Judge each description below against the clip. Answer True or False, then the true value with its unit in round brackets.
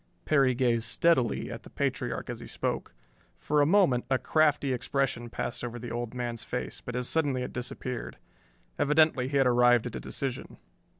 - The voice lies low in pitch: True (125 Hz)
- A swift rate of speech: False (180 wpm)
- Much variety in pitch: False (2.7 semitones)